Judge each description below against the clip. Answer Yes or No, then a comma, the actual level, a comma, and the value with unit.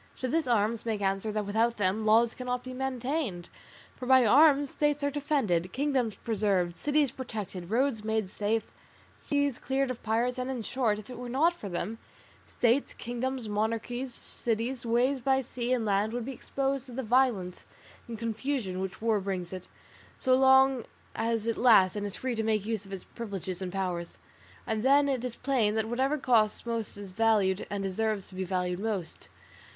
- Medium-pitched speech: No, high, 230 Hz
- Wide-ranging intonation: No, average, 4.1 semitones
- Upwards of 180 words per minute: Yes, average, 190 wpm